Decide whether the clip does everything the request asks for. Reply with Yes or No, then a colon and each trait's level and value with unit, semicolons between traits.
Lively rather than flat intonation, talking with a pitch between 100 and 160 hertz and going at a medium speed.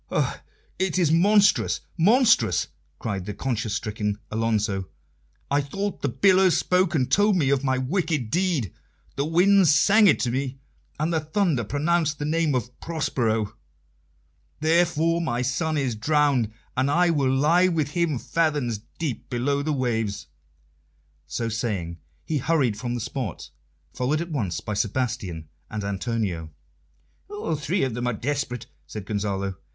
Yes: wide, 6.5 semitones; medium, 140 Hz; average, 150 wpm